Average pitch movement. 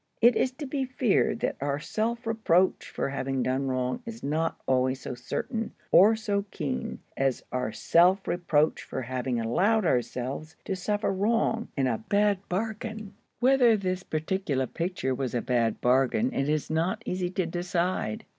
No: wide, 8.5 semitones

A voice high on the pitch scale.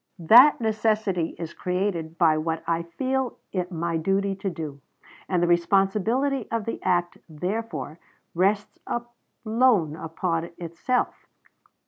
No: medium, 180 Hz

